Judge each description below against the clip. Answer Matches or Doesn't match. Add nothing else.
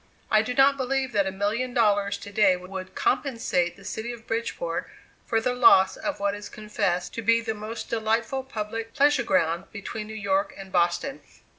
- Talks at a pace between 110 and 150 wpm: Doesn't match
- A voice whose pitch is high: Matches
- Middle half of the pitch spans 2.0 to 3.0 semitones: Doesn't match